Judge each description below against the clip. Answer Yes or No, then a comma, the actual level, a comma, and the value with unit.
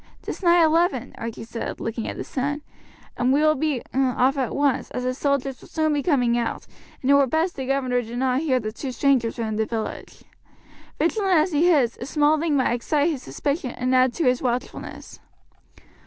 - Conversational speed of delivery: No, fast, 210 wpm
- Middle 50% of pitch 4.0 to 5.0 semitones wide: No, average, 3.5 semitones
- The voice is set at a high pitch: Yes, very high, 265 Hz